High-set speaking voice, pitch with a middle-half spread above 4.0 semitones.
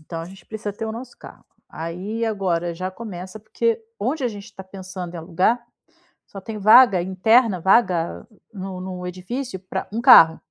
No: high, 195 Hz; average, 3.7 semitones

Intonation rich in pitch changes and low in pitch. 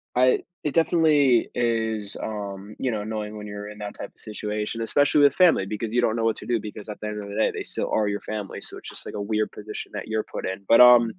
No: narrow, 2.4 semitones; low, 110 Hz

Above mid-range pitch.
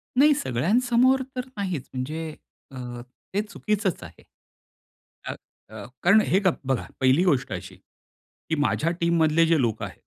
No: medium, 165 Hz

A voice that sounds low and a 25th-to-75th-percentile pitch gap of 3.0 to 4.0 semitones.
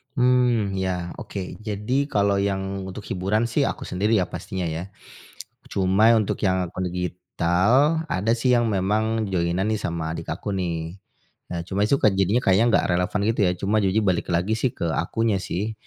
Yes: low, 100 Hz; average, 3.4 semitones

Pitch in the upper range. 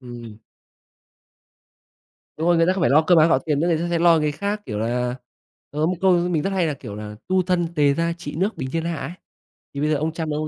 No: medium, 160 Hz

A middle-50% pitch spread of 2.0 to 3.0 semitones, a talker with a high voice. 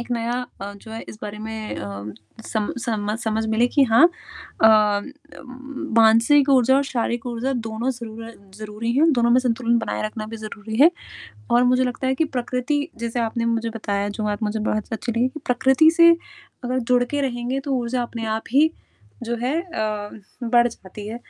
Yes: narrow, 2.5 semitones; high, 235 Hz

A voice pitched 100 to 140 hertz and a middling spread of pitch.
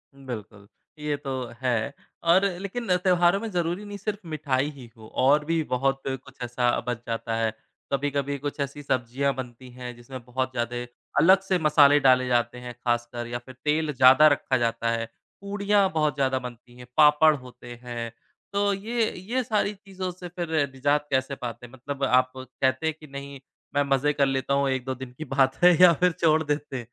Yes: low, 135 Hz; average, 4.2 semitones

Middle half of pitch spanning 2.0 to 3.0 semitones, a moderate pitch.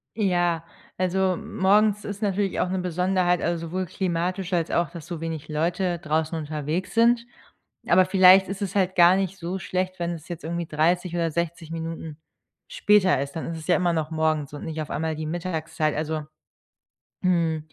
Yes: narrow, 2.6 semitones; medium, 175 Hz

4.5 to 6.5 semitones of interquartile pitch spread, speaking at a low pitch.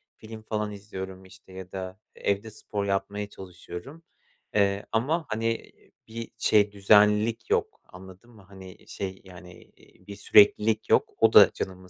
No: narrow, 2.5 semitones; low, 100 Hz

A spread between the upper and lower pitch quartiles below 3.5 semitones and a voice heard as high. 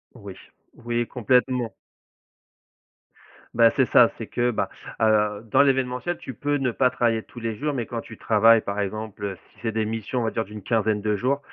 No: average, 2.7 semitones; low, 115 Hz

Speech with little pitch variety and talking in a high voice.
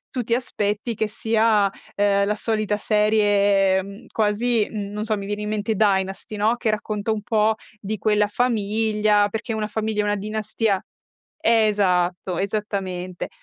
Yes: narrow, 1.5 semitones; high, 210 Hz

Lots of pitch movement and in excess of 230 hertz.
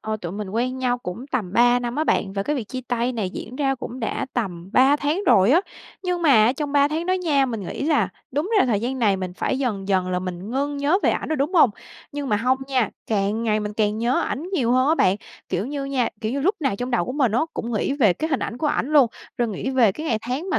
No: average, 4.8 semitones; very high, 250 Hz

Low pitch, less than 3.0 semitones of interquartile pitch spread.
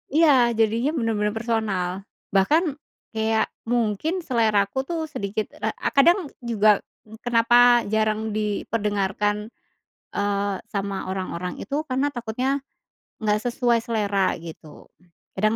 No: high, 215 Hz; narrow, 2.5 semitones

